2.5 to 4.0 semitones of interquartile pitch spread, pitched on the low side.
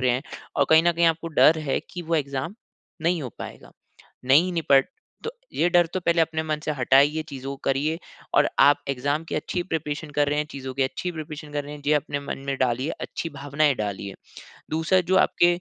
No: average, 3.0 semitones; medium, 150 Hz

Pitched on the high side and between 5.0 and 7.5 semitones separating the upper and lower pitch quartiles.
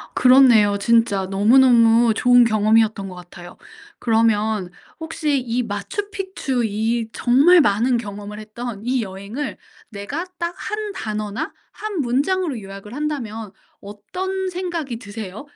Yes: high, 230 Hz; wide, 5.6 semitones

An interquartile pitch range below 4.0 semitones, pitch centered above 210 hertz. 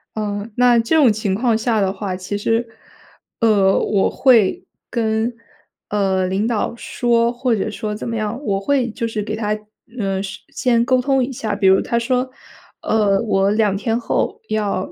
Yes: average, 2.8 semitones; high, 220 Hz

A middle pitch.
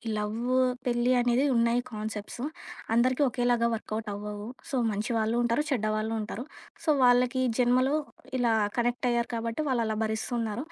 No: high, 235 Hz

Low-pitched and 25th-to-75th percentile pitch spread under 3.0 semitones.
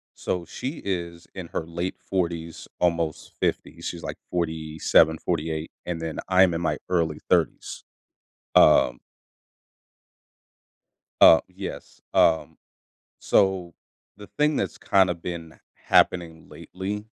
Yes: very low, 85 Hz; narrow, 2.4 semitones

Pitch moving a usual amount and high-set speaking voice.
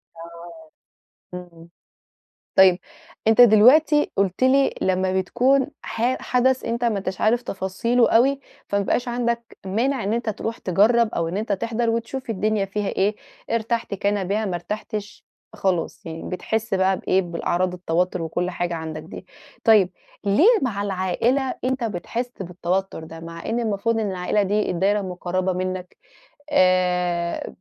Yes: average, 4.2 semitones; high, 200 Hz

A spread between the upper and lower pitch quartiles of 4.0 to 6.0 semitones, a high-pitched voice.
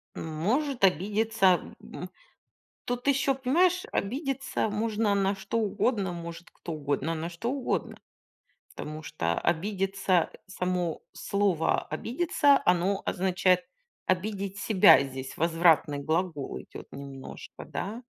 Yes: average, 5.1 semitones; high, 195 Hz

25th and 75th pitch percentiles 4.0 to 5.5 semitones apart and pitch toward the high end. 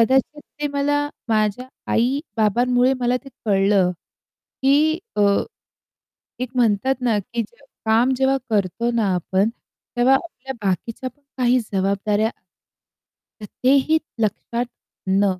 Yes: average, 4.3 semitones; high, 235 Hz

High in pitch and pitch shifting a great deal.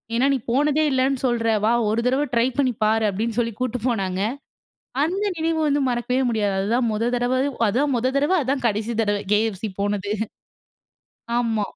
No: high, 240 Hz; average, 3.4 semitones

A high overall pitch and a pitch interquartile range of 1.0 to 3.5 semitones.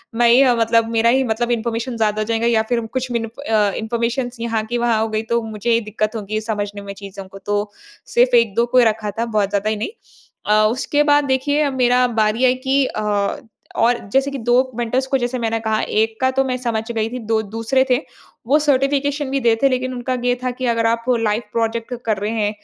Yes: high, 230 Hz; narrow, 2.6 semitones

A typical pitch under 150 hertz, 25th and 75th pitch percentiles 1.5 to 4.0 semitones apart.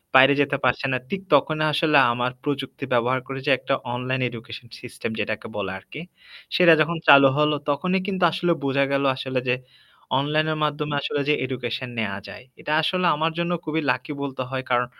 Yes: medium, 140 Hz; average, 3.4 semitones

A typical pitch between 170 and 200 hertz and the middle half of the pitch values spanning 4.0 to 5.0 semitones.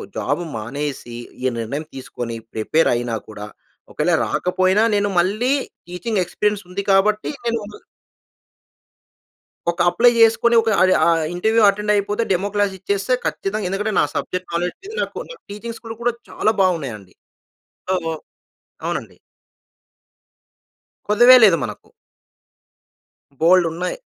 Yes: high, 190 Hz; average, 4.5 semitones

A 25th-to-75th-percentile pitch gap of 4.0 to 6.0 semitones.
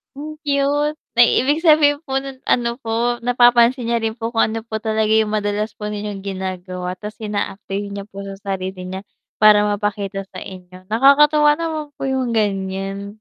Yes: average, 5.0 semitones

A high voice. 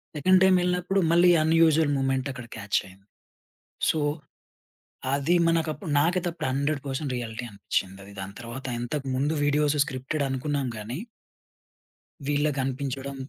No: medium, 140 Hz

